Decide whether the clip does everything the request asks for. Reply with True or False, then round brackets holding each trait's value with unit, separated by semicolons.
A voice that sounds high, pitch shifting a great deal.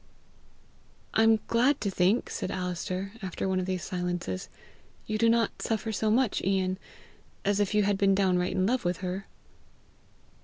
False (195 Hz; 2.9 semitones)